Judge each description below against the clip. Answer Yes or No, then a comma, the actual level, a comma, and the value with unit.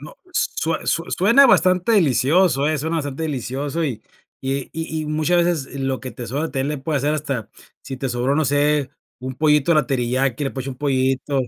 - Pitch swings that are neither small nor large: Yes, average, 3.1 semitones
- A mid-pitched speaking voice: Yes, medium, 145 Hz